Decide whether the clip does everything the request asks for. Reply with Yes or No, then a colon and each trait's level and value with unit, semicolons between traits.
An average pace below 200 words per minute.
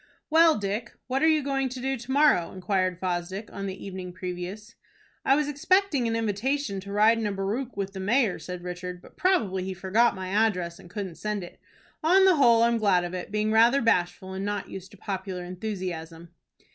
No: fast, 205 wpm